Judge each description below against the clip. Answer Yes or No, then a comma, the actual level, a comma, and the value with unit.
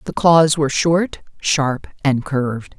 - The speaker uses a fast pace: No, average, 150 wpm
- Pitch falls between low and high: Yes, medium, 145 Hz